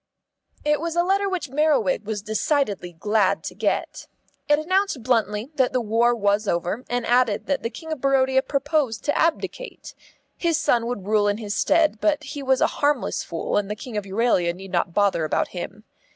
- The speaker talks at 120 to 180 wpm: No, average, 195 wpm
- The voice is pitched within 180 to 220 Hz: No, high, 240 Hz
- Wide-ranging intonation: Yes, wide, 6.1 semitones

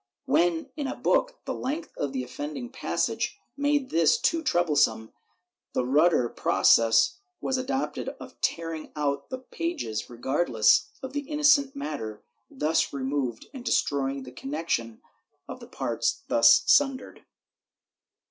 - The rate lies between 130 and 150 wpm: Yes, slow, 135 wpm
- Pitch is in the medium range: Yes, medium, 160 Hz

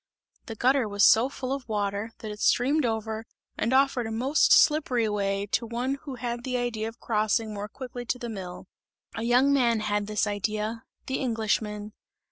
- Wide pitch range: No, average, 3.0 semitones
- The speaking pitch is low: No, high, 225 Hz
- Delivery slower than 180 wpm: No, average, 185 wpm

